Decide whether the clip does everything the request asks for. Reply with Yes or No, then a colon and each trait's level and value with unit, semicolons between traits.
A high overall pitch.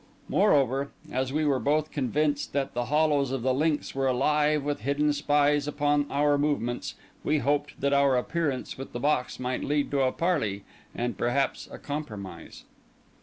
No: medium, 140 Hz